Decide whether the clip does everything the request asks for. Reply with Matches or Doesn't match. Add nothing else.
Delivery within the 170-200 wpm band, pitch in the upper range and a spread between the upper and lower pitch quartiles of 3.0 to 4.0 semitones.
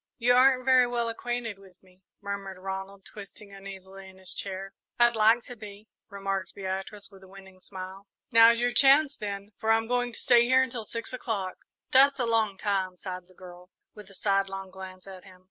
Matches